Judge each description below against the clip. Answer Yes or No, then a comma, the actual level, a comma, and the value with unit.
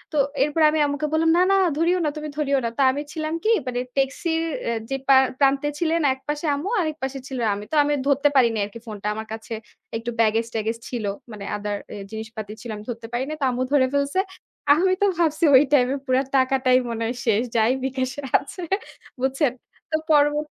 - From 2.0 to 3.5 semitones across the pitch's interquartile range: No, average, 4.3 semitones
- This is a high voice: Yes, very high, 270 Hz